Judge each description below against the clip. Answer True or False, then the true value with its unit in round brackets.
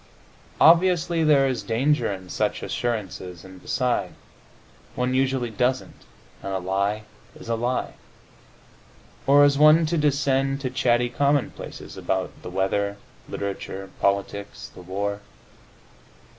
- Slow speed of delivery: True (120 wpm)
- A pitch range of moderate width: False (5.8 semitones)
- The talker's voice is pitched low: True (120 Hz)